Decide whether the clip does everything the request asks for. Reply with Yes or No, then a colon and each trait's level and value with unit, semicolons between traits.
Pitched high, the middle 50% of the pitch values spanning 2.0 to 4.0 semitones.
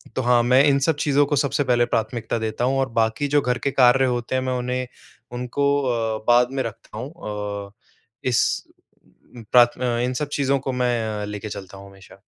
No: low, 125 Hz; average, 2.9 semitones